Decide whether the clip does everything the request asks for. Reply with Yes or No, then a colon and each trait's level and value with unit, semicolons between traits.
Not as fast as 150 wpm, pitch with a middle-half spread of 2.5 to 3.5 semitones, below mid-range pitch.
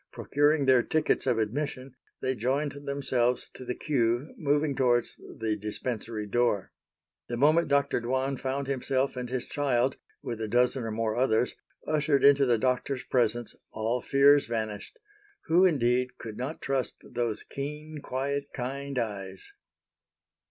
Yes: average, 140 wpm; average, 3.0 semitones; low, 130 Hz